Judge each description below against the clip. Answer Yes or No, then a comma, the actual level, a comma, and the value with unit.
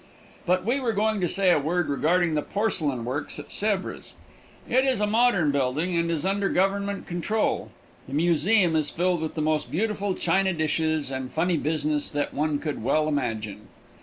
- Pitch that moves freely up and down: No, average, 4.7 semitones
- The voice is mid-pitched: Yes, medium, 170 Hz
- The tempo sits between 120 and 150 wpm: No, average, 180 wpm